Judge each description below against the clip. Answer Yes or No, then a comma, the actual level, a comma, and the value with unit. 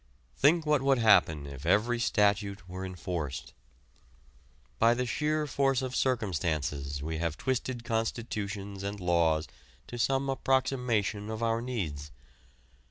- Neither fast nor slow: No, slow, 125 wpm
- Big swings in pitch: Yes, wide, 6.5 semitones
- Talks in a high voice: No, low, 105 Hz